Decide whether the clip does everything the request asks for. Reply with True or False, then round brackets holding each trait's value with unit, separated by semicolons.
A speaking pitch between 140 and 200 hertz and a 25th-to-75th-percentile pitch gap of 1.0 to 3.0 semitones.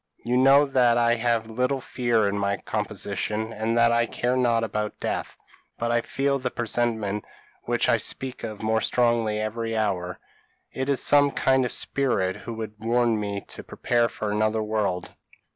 False (115 Hz; 2.4 semitones)